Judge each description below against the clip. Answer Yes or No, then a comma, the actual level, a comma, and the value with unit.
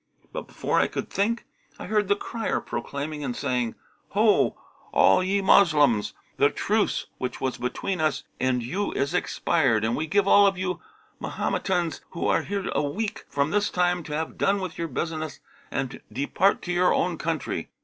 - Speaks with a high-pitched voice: No, medium, 165 Hz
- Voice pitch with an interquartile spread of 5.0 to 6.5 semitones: Yes, wide, 5.5 semitones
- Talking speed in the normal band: Yes, average, 180 wpm